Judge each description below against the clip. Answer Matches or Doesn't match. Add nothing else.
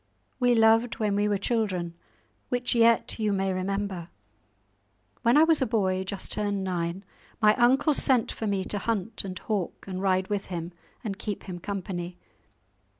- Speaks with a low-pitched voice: Doesn't match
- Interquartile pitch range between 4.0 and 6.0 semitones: Doesn't match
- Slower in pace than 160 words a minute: Doesn't match